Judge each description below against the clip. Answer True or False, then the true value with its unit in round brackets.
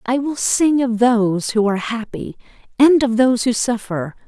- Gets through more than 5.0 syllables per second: False (4.9 syllables/s)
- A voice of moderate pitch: False (235 Hz)